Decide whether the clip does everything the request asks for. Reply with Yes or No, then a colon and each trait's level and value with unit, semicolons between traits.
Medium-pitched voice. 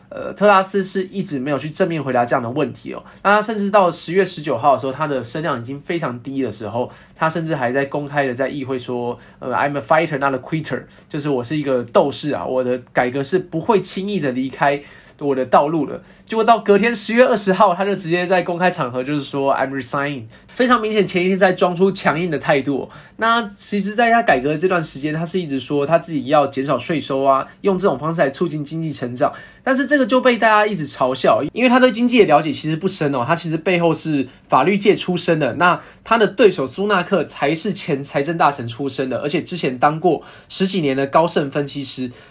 Yes: medium, 160 Hz